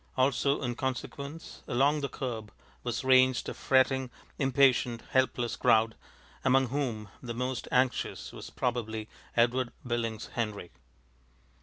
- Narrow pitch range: Yes, narrow, 2.1 semitones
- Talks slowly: Yes, slow, 120 wpm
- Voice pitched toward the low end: Yes, low, 125 Hz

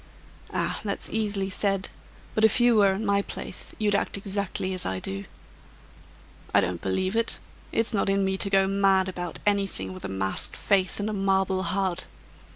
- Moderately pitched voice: No, high, 195 Hz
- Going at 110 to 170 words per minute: No, average, 180 wpm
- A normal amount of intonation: No, narrow, 1.4 semitones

